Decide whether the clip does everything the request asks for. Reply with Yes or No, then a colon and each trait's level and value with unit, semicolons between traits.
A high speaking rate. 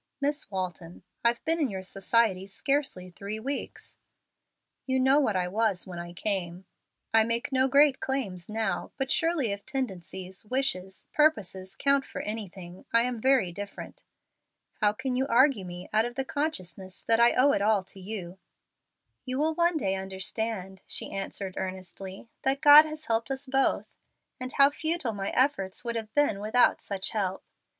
No: average, 170 wpm